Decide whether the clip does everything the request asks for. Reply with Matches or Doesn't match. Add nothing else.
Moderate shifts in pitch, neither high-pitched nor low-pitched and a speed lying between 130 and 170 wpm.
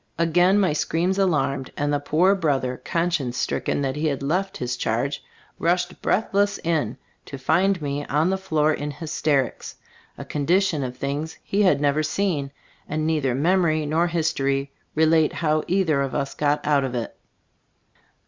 Matches